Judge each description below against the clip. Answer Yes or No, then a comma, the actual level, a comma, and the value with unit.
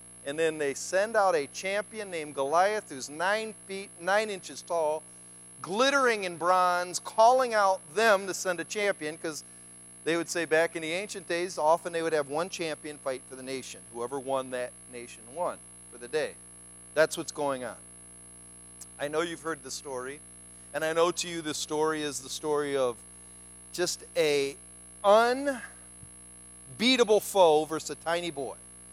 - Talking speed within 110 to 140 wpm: No, average, 170 wpm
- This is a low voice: No, medium, 155 Hz